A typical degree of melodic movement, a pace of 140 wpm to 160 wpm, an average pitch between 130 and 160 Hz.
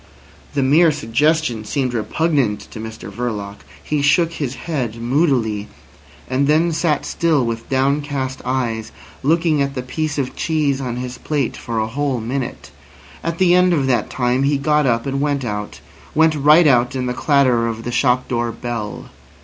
No: average, 4.0 semitones; average, 170 wpm; low, 135 Hz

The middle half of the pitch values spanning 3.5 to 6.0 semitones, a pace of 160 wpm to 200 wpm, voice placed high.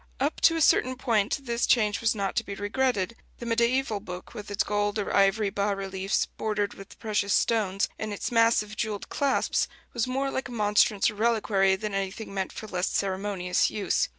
No: average, 2.9 semitones; average, 190 wpm; high, 210 Hz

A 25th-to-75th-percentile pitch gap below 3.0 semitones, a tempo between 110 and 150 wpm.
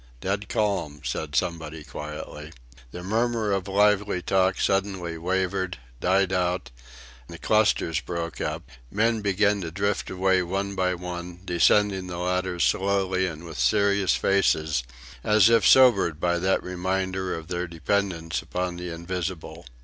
Yes: narrow, 2.4 semitones; average, 140 wpm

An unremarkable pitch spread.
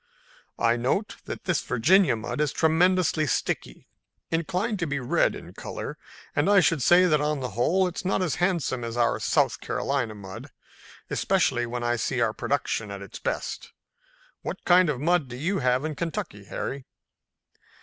No: wide, 6.7 semitones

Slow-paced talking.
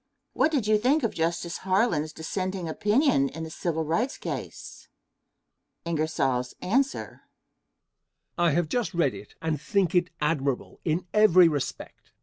Yes: slow, 130 wpm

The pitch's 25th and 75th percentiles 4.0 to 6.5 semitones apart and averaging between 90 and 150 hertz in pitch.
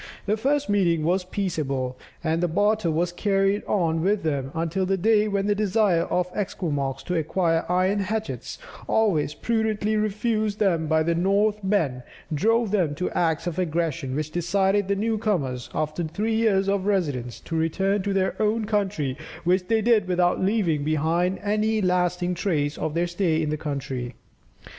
No: average, 4.4 semitones; medium, 185 Hz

